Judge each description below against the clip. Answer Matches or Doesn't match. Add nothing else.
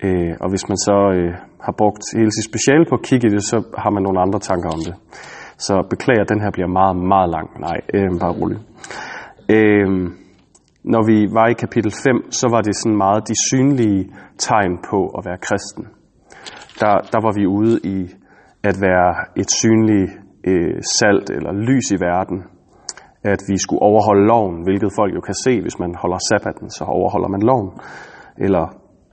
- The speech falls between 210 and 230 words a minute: Doesn't match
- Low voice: Matches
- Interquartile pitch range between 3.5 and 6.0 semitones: Doesn't match